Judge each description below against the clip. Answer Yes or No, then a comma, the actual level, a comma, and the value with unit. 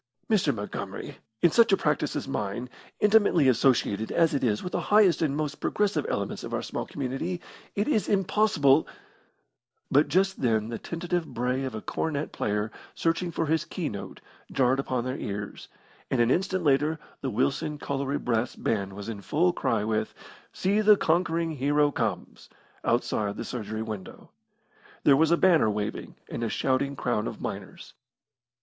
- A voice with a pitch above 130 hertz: Yes, medium, 140 Hz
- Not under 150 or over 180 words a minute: Yes, average, 170 wpm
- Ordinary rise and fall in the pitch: No, wide, 6.7 semitones